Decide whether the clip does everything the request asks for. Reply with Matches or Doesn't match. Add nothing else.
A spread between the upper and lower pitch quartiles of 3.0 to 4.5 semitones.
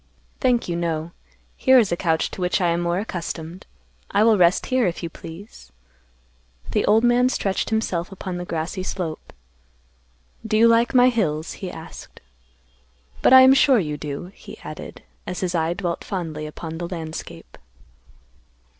Doesn't match